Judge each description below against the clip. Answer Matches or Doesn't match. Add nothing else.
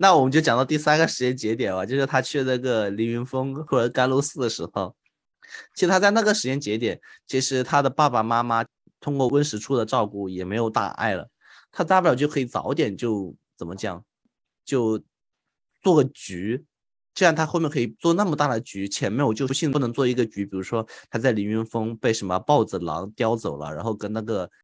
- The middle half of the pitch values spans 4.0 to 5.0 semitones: Matches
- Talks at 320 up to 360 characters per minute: Doesn't match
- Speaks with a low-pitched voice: Matches